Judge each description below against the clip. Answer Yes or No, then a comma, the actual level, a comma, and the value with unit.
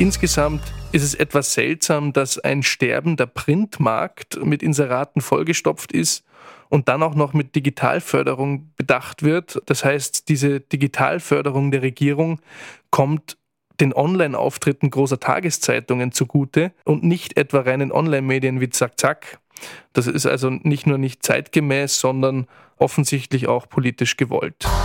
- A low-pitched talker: No, medium, 145 Hz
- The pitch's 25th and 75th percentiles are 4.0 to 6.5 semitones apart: No, narrow, 2.5 semitones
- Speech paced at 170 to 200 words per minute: No, average, 130 wpm